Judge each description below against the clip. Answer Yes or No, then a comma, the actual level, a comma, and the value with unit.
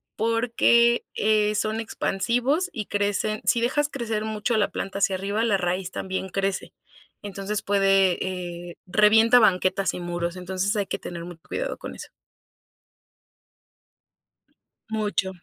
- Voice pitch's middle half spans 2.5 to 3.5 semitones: Yes, average, 2.9 semitones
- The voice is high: Yes, high, 205 Hz